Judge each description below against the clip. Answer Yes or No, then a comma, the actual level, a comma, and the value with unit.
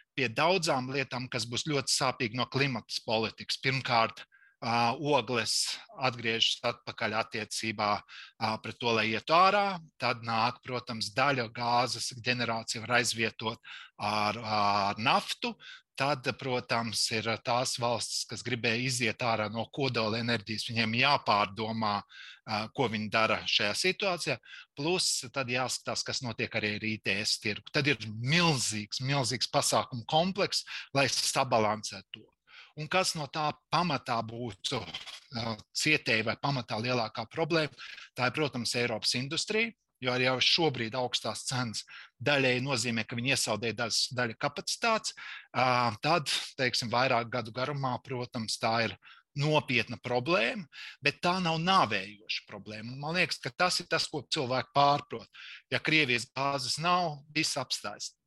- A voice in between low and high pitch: No, low, 125 Hz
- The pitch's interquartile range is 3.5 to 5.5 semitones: Yes, average, 4.1 semitones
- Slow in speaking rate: Yes, slow, 130 wpm